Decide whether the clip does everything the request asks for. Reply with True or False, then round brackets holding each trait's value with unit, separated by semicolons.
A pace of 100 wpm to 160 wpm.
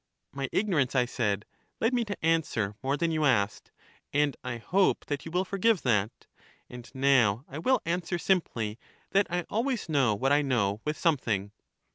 False (175 wpm)